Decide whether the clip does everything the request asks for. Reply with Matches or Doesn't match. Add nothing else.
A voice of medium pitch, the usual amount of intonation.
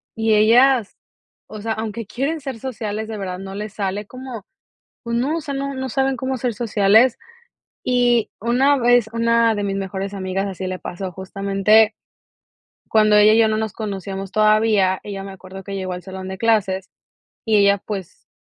Doesn't match